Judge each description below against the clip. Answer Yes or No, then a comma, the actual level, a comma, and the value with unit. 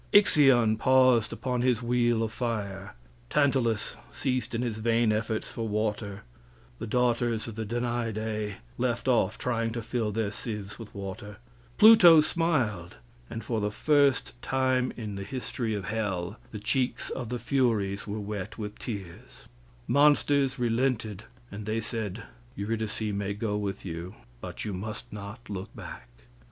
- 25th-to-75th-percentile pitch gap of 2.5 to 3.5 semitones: Yes, average, 3.1 semitones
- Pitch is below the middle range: Yes, low, 115 Hz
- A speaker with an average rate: Yes, average, 150 wpm